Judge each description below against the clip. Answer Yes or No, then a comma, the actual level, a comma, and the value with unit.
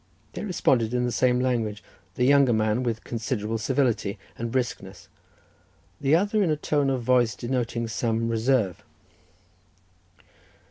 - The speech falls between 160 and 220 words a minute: No, slow, 135 wpm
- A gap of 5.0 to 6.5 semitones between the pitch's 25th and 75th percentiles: No, average, 2.7 semitones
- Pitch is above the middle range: No, low, 120 Hz